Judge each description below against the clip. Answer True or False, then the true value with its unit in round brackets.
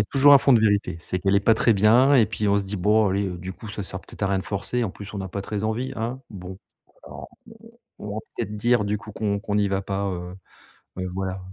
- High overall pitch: False (100 Hz)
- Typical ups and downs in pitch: False (2.2 semitones)